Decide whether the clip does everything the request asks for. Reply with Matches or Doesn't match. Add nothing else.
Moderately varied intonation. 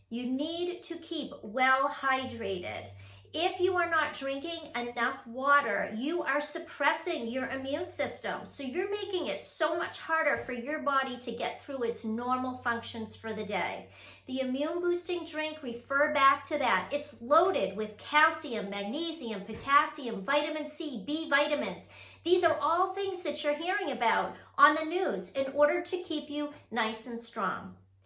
Matches